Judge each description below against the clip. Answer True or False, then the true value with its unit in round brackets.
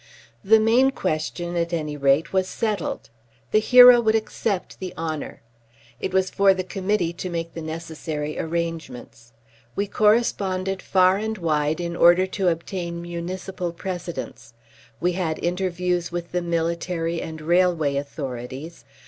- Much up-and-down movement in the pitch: False (2.7 semitones)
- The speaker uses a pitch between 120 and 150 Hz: False (175 Hz)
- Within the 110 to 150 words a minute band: True (140 wpm)